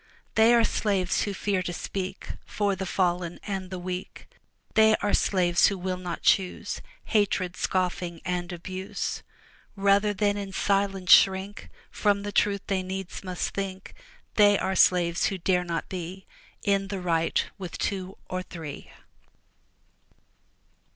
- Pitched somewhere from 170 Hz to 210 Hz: Yes, high, 190 Hz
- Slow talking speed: No, average, 145 wpm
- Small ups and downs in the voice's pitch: Yes, narrow, 1.9 semitones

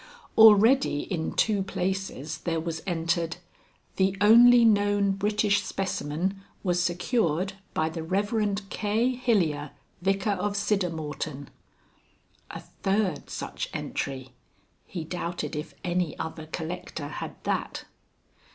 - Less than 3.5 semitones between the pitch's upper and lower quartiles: No, average, 4.1 semitones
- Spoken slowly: Yes, slow, 110 wpm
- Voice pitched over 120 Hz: Yes, medium, 185 Hz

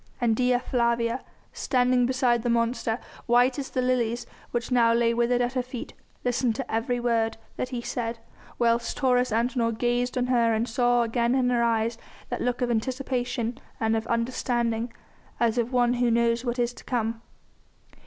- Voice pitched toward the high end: Yes, high, 240 Hz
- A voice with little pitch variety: Yes, narrow, 1.2 semitones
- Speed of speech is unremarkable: Yes, average, 175 wpm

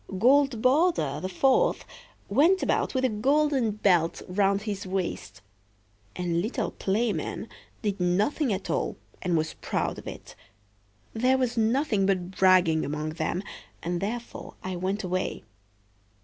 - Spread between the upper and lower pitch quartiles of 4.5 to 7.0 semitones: Yes, wide, 5.5 semitones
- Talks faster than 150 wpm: No, slow, 135 wpm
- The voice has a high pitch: Yes, high, 200 Hz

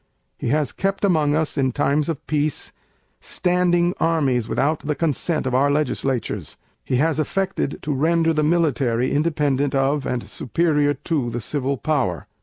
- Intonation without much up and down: No, average, 3.2 semitones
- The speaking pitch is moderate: Yes, medium, 150 Hz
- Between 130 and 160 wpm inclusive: Yes, average, 155 wpm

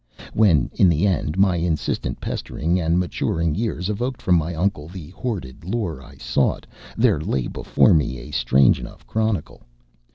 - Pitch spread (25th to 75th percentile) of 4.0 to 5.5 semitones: Yes, average, 4.5 semitones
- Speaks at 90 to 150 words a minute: No, average, 160 wpm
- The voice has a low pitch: Yes, very low, 85 Hz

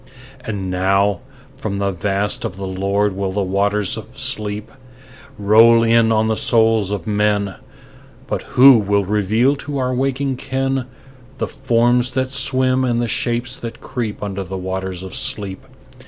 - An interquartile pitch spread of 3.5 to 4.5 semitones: Yes, average, 3.9 semitones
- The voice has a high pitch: No, low, 105 Hz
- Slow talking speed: No, average, 155 wpm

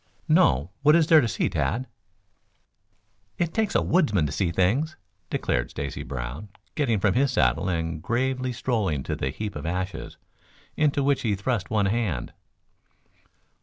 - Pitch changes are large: Yes, wide, 8.1 semitones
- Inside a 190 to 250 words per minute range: No, average, 155 wpm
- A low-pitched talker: Yes, low, 105 Hz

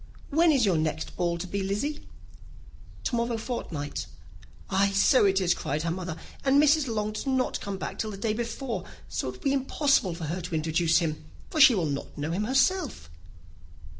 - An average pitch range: No, wide, 7.4 semitones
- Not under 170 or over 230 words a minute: Yes, average, 195 wpm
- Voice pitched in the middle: No, high, 200 Hz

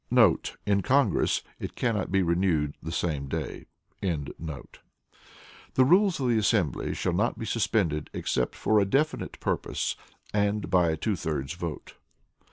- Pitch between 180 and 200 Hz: No, very low, 90 Hz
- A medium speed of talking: Yes, average, 145 wpm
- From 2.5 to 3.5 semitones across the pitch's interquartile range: No, wide, 5.5 semitones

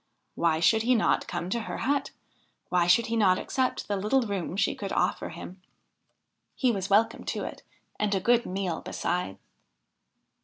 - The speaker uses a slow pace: No, average, 170 wpm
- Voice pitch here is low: No, high, 200 Hz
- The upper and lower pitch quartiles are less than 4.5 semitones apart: Yes, average, 4.1 semitones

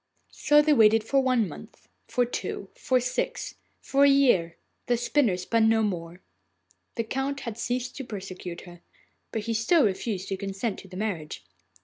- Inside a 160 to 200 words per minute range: Yes, average, 170 wpm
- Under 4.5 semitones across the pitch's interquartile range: No, average, 5.0 semitones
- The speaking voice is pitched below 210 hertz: No, high, 225 Hz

